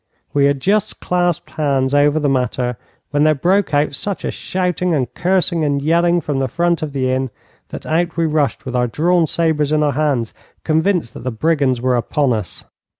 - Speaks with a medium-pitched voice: Yes, medium, 150 Hz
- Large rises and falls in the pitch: No, average, 4.2 semitones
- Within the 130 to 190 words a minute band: No, average, 200 wpm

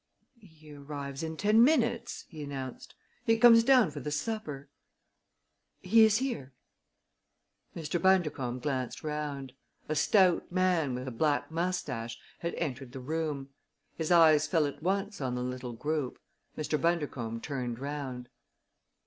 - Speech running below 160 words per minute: Yes, average, 140 wpm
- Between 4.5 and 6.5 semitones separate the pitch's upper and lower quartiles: Yes, average, 4.8 semitones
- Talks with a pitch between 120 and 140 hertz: No, medium, 150 Hz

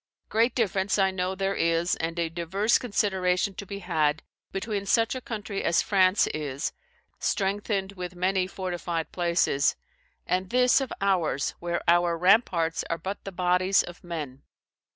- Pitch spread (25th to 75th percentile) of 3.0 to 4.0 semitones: No, narrow, 2.6 semitones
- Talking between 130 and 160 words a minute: Yes, average, 150 wpm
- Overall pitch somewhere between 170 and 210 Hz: Yes, medium, 185 Hz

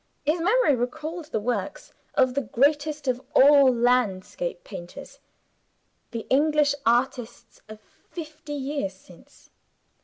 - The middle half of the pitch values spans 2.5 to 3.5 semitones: No, average, 4.2 semitones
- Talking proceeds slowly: Yes, slow, 115 wpm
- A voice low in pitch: No, very high, 270 Hz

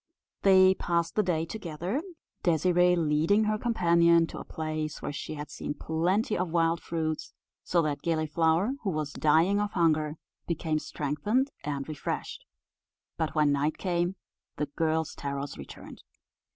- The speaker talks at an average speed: Yes, average, 145 wpm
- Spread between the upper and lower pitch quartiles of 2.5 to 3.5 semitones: Yes, average, 2.8 semitones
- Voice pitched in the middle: Yes, medium, 165 Hz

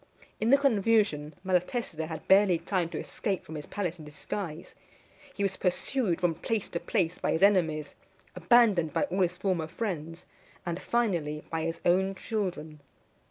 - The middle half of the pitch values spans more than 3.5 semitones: Yes, average, 3.9 semitones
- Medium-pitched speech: Yes, medium, 180 Hz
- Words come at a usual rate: Yes, average, 160 wpm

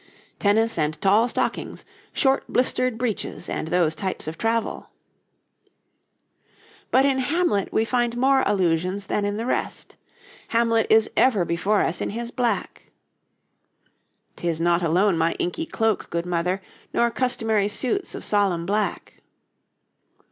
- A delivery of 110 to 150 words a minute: Yes, slow, 135 wpm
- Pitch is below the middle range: No, high, 210 Hz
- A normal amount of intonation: Yes, average, 5.0 semitones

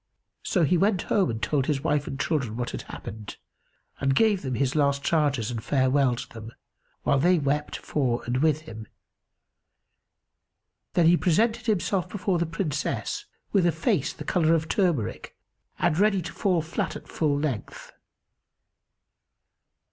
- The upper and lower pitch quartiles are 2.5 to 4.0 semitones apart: No, average, 5.0 semitones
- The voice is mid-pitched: Yes, medium, 150 Hz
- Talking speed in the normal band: Yes, average, 155 wpm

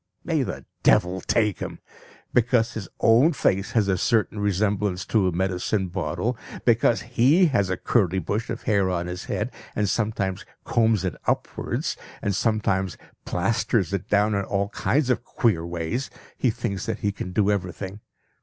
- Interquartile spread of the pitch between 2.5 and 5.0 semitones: Yes, average, 3.3 semitones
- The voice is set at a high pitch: No, low, 100 Hz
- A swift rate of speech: No, average, 165 wpm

